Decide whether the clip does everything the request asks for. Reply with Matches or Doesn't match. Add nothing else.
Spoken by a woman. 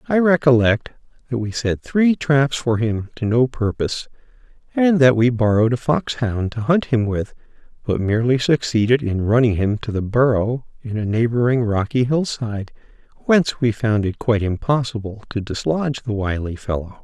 Doesn't match